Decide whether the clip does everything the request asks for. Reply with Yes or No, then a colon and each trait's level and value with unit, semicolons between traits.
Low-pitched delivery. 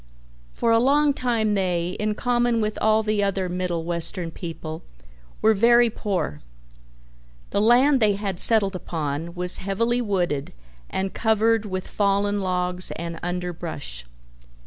No: high, 195 Hz